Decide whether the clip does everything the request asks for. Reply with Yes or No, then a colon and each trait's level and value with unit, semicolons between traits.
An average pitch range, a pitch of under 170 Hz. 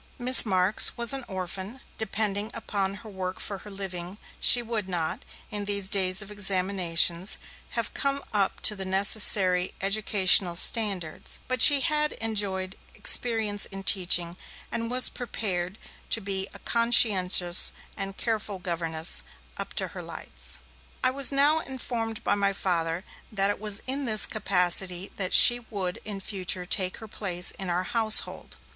No: average, 3.2 semitones; high, 200 Hz